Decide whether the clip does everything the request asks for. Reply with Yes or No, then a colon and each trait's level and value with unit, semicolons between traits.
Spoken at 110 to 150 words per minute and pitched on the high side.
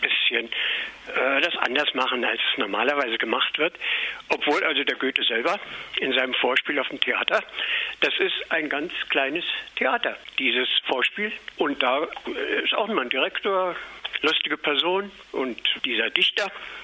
Yes: average, 145 wpm; very high, 395 Hz